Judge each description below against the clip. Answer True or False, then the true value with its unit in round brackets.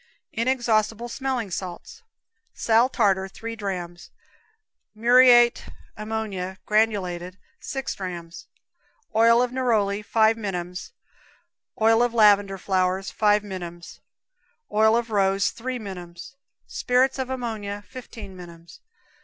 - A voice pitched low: False (210 Hz)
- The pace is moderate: False (90 wpm)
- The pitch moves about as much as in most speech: True (3.6 semitones)